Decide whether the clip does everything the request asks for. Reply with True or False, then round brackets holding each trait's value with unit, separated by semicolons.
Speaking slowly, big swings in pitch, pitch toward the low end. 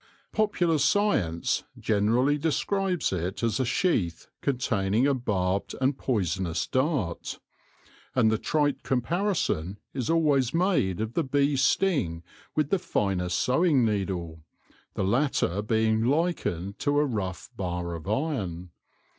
True (125 wpm; 7.6 semitones; 120 Hz)